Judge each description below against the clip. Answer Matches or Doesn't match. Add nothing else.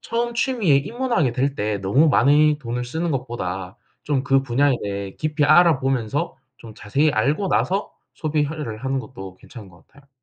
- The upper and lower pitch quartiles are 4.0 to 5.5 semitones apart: Matches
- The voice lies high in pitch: Doesn't match